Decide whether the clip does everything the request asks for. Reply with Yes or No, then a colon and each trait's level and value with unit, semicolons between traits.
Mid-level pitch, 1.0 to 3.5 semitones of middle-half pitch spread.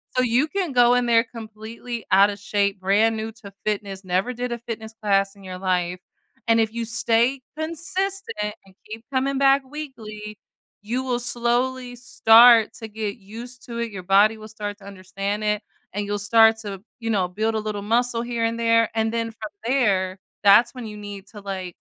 No: high, 225 Hz; average, 2.9 semitones